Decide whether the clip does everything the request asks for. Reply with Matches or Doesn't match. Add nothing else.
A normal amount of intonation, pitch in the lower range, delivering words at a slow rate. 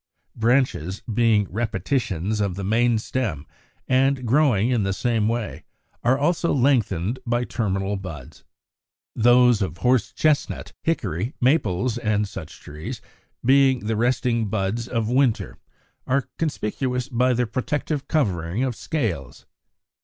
Matches